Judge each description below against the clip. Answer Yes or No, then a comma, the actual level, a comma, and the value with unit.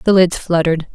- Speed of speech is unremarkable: Yes, average, 190 wpm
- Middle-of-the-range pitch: Yes, medium, 170 Hz